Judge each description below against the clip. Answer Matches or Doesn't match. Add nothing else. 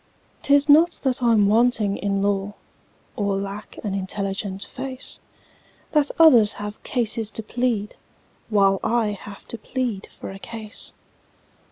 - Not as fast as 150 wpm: Matches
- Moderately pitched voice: Doesn't match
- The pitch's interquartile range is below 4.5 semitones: Matches